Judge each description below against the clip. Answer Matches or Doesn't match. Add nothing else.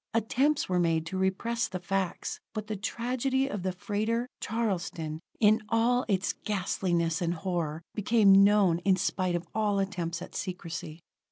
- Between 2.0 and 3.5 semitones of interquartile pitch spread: Doesn't match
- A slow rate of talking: Doesn't match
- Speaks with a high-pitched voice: Matches